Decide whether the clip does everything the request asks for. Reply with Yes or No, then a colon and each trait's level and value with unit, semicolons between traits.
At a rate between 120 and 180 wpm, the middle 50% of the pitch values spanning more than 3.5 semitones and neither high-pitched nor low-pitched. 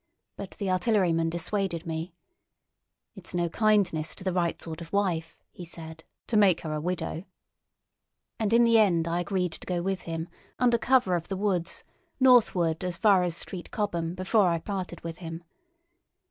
No: average, 175 wpm; average, 3.2 semitones; medium, 180 Hz